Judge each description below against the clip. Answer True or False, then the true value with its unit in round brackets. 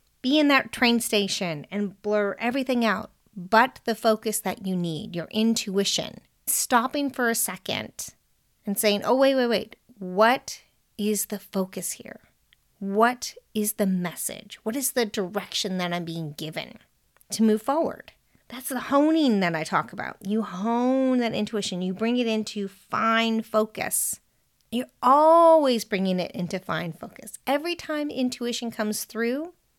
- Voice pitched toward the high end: True (220 Hz)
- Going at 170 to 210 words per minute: False (155 wpm)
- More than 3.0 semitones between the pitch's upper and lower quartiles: True (3.7 semitones)